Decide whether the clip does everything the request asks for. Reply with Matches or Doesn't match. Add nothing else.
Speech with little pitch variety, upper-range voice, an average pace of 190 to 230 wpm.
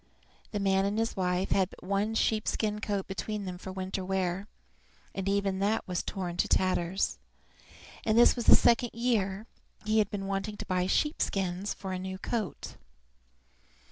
Doesn't match